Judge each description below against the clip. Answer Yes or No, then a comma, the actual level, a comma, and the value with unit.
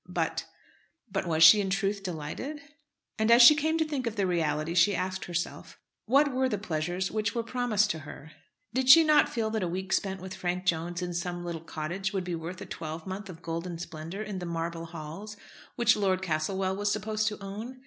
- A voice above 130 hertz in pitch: Yes, high, 190 Hz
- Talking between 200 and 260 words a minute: Yes, fast, 205 wpm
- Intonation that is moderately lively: Yes, average, 4.0 semitones